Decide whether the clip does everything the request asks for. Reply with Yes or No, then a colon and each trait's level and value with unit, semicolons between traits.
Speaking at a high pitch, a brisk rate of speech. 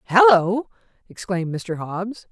No: high, 200 Hz; slow, 105 wpm